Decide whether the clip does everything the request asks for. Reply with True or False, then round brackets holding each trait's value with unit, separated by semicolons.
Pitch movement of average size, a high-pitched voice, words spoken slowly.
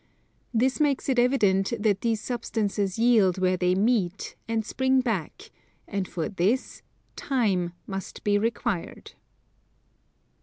True (4.3 semitones; 215 Hz; 120 wpm)